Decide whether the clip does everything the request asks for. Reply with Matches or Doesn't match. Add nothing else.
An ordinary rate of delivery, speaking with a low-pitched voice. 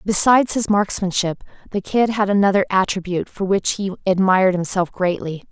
Doesn't match